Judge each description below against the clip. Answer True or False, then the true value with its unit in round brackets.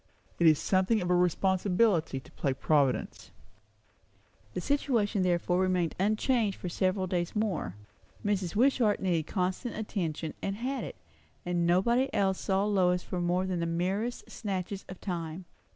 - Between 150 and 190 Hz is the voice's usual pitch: True (185 Hz)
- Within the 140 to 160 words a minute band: True (150 wpm)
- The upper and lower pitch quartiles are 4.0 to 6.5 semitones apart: False (2.9 semitones)